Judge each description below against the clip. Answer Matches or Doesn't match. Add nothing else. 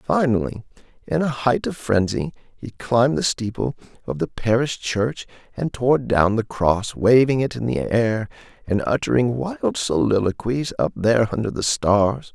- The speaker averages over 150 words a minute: Matches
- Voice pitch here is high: Doesn't match